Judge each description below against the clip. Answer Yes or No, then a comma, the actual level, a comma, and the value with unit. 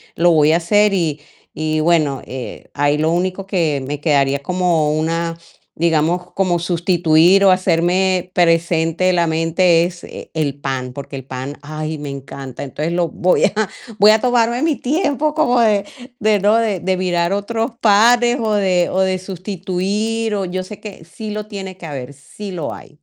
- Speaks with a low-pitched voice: No, medium, 175 Hz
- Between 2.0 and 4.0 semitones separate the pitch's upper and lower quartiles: No, average, 4.4 semitones